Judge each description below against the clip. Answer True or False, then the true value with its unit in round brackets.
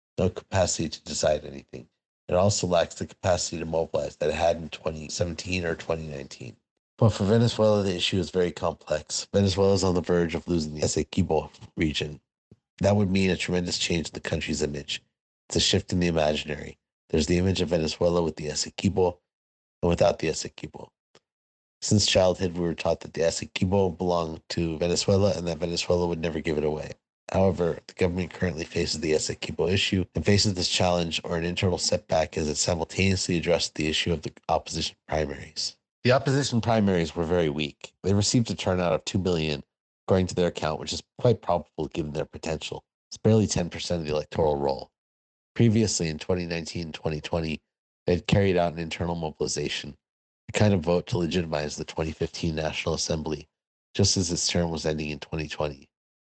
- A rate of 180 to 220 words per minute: True (185 wpm)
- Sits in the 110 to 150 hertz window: False (85 Hz)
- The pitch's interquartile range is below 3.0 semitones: False (3.5 semitones)